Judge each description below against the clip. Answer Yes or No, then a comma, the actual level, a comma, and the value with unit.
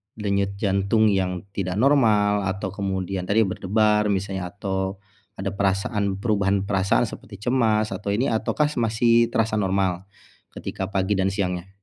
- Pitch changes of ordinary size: No, narrow, 2.0 semitones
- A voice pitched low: Yes, low, 100 Hz